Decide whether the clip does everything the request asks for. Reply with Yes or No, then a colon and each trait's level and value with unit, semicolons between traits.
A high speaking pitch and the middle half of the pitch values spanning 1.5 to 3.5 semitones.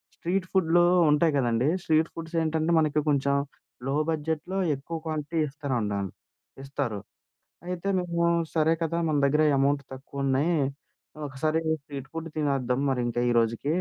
No: medium, 150 Hz; average, 3.2 semitones